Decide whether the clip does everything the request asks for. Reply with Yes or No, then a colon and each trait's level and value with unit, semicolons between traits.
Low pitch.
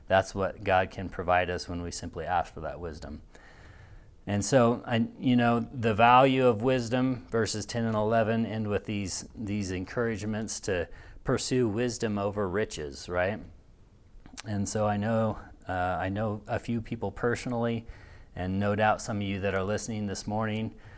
Yes: low, 105 Hz